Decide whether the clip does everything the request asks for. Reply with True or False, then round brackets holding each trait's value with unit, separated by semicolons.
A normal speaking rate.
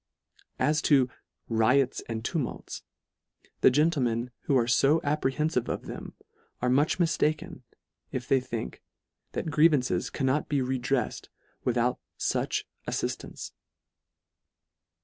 False (120 wpm)